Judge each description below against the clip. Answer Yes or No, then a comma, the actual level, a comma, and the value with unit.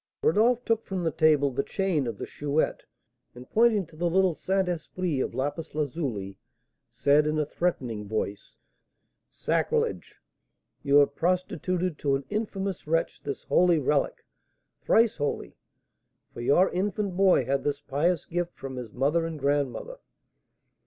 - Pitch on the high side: No, medium, 155 Hz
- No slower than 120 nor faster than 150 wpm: Yes, average, 145 wpm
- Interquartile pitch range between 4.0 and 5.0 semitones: Yes, average, 4.7 semitones